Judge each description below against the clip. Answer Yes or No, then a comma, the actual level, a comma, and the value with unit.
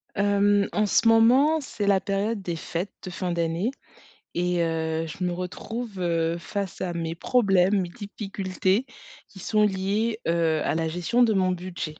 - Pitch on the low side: No, high, 190 Hz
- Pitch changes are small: No, average, 3.3 semitones